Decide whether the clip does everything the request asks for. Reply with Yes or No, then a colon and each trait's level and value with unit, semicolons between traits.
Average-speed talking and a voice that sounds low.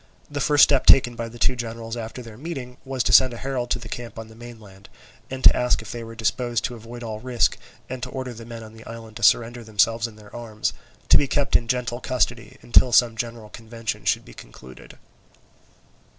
No: fast, 220 wpm; low, 115 Hz